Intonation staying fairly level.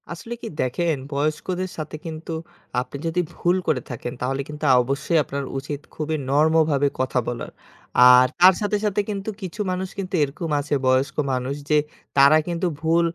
No: average, 4.0 semitones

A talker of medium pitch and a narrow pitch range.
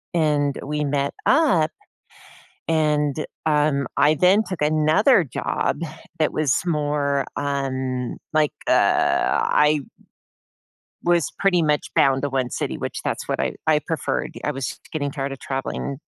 Yes: medium, 150 Hz; narrow, 2.0 semitones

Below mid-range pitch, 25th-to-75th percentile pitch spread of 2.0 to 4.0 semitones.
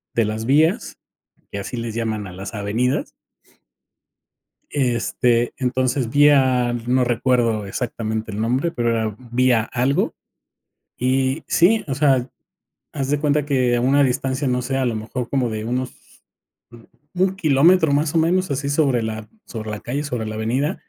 Yes: low, 125 Hz; average, 3.7 semitones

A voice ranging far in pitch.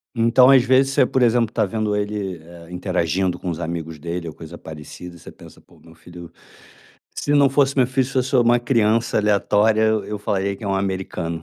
Yes: wide, 5.7 semitones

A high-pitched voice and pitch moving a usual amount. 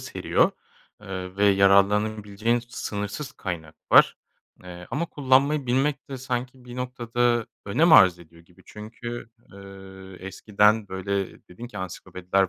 No: low, 105 Hz; average, 4.3 semitones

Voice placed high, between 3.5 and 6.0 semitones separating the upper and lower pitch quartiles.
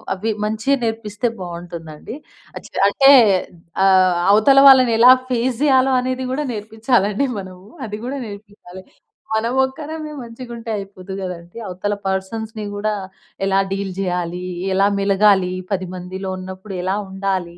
Yes: high, 205 Hz; average, 4.0 semitones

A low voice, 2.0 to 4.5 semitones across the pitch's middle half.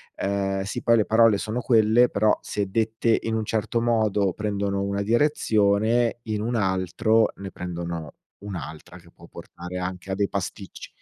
Yes: low, 100 Hz; average, 2.7 semitones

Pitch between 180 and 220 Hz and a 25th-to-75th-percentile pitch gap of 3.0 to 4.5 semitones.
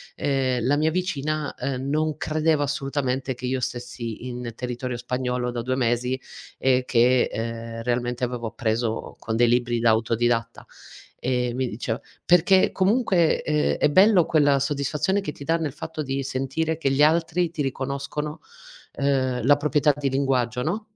No: low, 135 Hz; average, 3.6 semitones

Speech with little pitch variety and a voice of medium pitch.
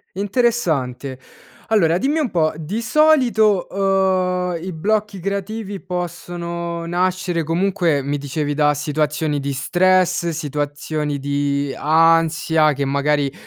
No: average, 4.4 semitones; medium, 170 Hz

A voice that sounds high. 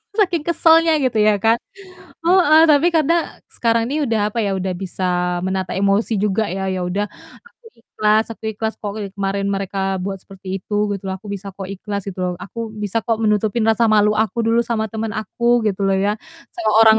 Yes: high, 215 Hz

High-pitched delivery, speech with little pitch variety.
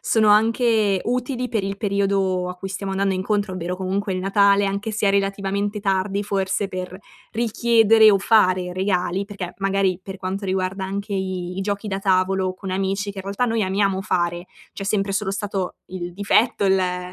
Yes: high, 195 Hz; narrow, 1.6 semitones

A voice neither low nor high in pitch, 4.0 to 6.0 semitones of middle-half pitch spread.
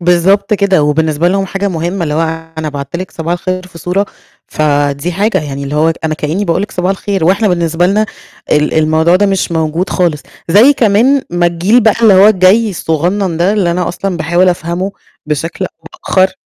No: medium, 175 Hz; average, 3.4 semitones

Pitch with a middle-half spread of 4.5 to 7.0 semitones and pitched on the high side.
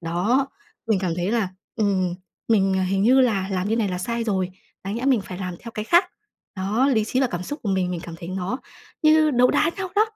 Yes: average, 4.8 semitones; high, 205 Hz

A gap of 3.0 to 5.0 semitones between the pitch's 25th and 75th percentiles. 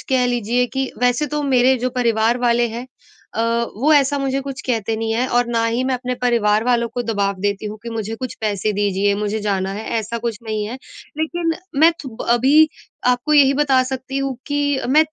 Yes: average, 3.3 semitones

